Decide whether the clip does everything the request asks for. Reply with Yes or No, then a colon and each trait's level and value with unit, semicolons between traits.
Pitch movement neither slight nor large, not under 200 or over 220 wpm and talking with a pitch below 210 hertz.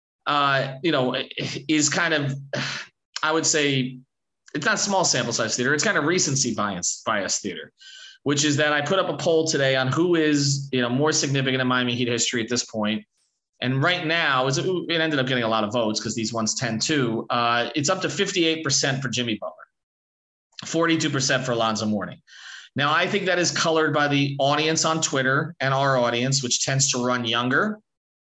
Yes: average, 4.5 semitones; fast, 205 wpm; medium, 140 Hz